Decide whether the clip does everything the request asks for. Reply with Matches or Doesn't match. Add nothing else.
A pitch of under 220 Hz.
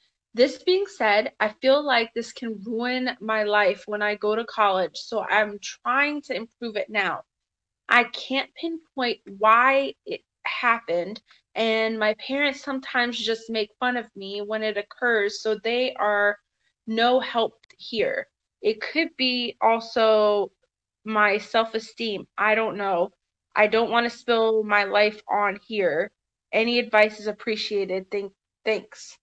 Doesn't match